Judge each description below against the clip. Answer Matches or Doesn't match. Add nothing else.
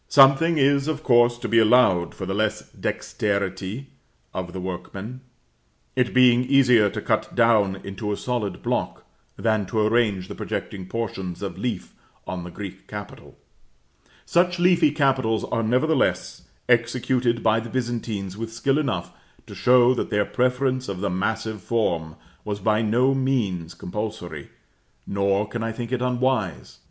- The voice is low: Matches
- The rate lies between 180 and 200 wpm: Doesn't match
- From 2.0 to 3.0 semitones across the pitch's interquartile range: Doesn't match